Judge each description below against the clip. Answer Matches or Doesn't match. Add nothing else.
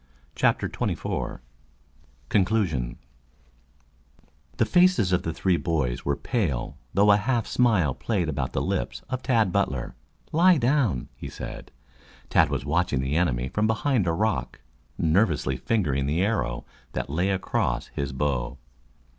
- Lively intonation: Matches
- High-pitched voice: Doesn't match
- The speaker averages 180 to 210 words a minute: Doesn't match